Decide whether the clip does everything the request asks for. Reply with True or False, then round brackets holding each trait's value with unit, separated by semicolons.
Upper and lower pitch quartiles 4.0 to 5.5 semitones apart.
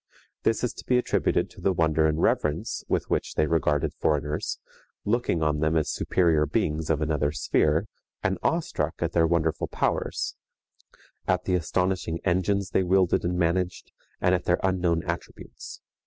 False (2.9 semitones)